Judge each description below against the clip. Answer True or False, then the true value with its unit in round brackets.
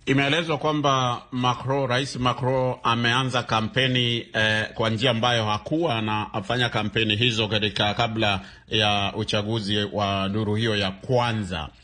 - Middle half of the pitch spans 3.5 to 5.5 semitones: False (2.8 semitones)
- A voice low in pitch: True (115 Hz)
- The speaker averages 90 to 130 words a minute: True (125 wpm)